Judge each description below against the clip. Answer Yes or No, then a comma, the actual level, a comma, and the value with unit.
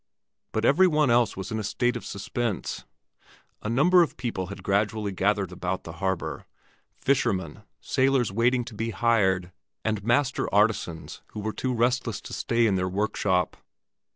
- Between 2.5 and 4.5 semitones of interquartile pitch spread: Yes, average, 4.0 semitones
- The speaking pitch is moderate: No, low, 110 Hz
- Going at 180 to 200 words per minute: No, average, 160 wpm